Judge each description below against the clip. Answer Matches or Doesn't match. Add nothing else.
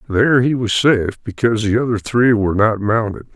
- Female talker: Doesn't match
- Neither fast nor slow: Matches